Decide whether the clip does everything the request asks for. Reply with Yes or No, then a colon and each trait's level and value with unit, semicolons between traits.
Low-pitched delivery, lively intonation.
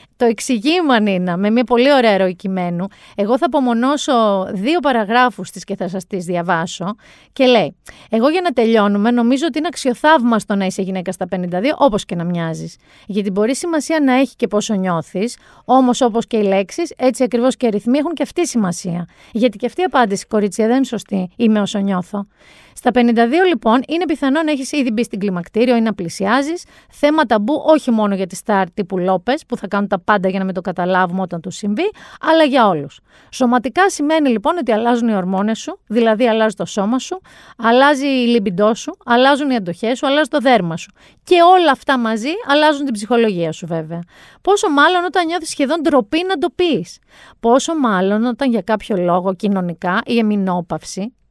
No: high, 230 Hz; wide, 6.2 semitones